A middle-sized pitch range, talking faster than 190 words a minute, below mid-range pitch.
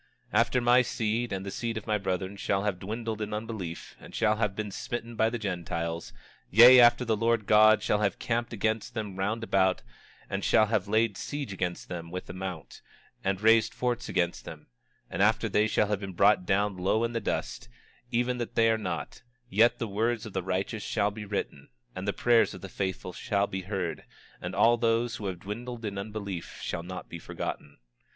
Yes: average, 3.2 semitones; fast, 205 wpm; low, 105 Hz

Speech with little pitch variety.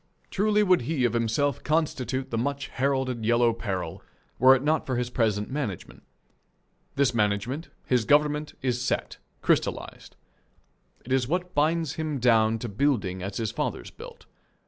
No: average, 4.2 semitones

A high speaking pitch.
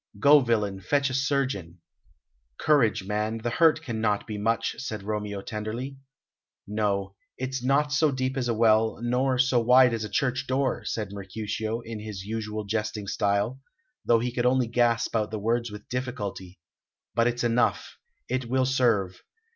No: low, 115 Hz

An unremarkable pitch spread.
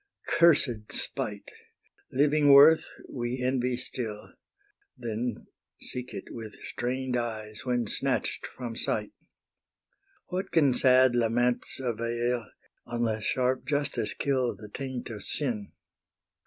No: narrow, 2.2 semitones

